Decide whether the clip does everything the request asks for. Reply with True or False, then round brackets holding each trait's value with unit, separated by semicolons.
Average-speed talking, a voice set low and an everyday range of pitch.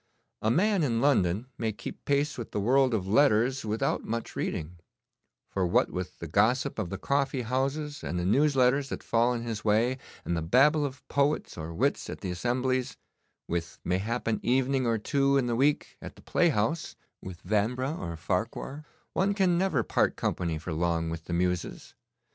False (185 wpm; 120 Hz; 7.1 semitones)